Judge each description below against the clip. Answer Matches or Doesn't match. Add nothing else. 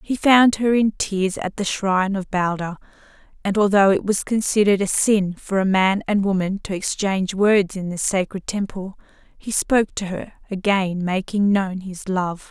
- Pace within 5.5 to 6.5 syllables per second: Doesn't match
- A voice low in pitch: Doesn't match